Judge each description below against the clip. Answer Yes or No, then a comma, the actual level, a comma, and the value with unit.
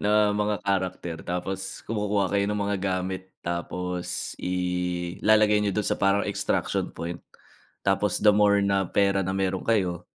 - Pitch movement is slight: Yes, narrow, 2.3 semitones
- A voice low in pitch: Yes, very low, 95 Hz